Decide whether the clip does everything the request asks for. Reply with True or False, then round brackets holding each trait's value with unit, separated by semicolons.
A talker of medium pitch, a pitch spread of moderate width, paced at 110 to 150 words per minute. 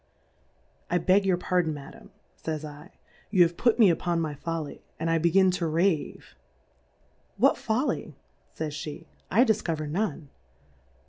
True (170 Hz; 3.6 semitones; 140 wpm)